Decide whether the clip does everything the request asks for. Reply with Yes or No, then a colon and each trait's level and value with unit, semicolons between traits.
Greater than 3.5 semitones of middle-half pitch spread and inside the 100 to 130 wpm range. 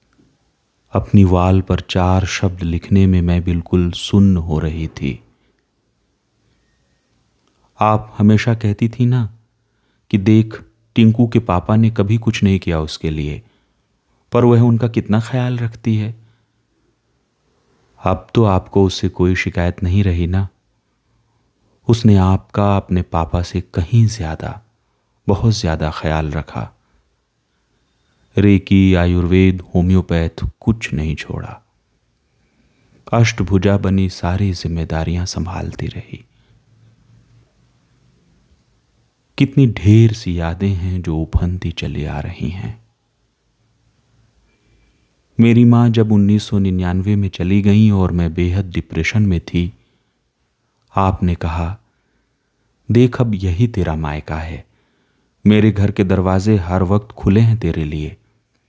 Yes: average, 4.2 semitones; average, 115 wpm